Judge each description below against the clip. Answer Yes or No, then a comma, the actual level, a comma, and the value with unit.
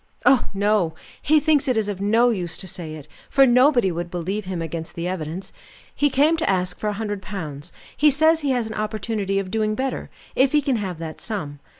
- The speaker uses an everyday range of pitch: No, wide, 6.1 semitones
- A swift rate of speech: Yes, fast, 220 wpm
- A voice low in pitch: No, high, 205 Hz